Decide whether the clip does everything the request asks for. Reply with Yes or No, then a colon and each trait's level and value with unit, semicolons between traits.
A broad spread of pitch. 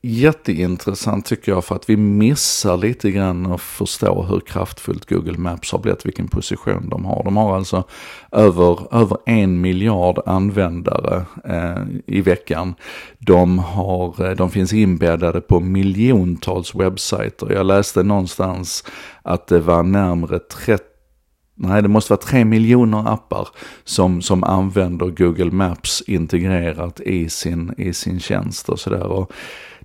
No: average, 2.7 semitones